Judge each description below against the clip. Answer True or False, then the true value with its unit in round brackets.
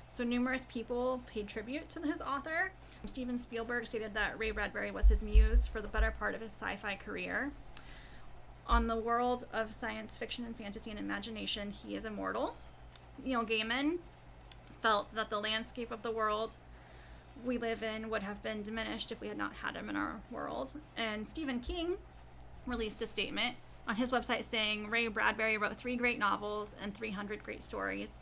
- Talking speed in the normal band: True (180 wpm)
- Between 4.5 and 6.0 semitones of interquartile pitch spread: False (2.4 semitones)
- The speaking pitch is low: False (225 Hz)